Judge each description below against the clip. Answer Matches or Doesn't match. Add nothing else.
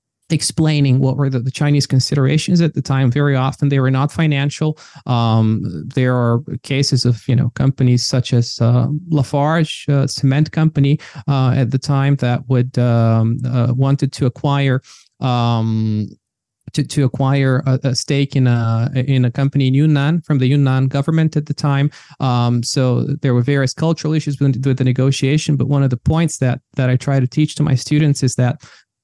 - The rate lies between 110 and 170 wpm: Doesn't match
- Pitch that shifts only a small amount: Matches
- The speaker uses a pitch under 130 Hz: Doesn't match